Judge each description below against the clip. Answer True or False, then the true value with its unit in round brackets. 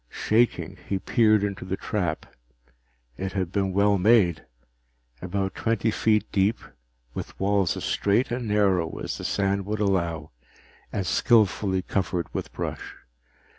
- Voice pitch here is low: True (100 Hz)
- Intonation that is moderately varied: False (2.3 semitones)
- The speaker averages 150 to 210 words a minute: False (135 wpm)